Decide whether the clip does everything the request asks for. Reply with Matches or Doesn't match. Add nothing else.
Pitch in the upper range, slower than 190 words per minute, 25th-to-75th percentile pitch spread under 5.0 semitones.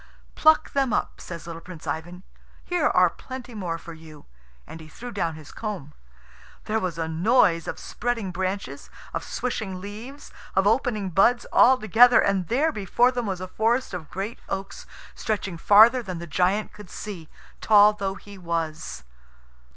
Doesn't match